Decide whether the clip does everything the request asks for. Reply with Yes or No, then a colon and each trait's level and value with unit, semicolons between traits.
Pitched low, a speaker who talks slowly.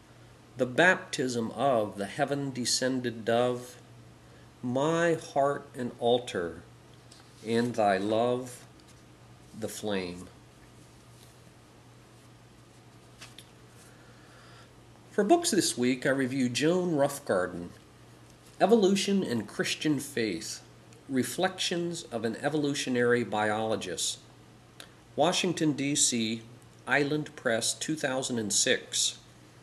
Yes: low, 120 Hz; slow, 75 wpm